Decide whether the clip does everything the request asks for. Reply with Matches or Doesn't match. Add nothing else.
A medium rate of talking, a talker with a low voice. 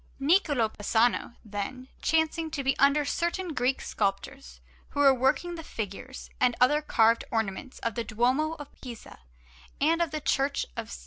Doesn't match